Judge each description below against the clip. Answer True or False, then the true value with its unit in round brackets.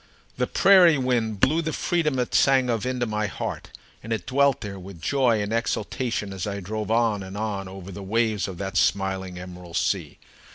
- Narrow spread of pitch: False (4.6 semitones)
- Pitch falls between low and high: False (105 Hz)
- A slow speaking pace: False (195 wpm)